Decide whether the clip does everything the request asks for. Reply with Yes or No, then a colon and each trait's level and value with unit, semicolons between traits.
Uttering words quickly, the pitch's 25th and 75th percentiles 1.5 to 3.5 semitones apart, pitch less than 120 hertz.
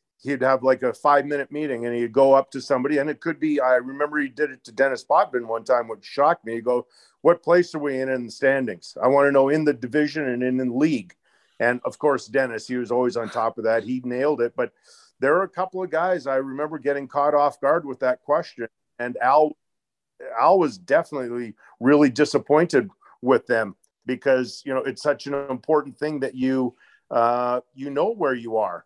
No: fast, 220 wpm; average, 2.8 semitones; low, 135 Hz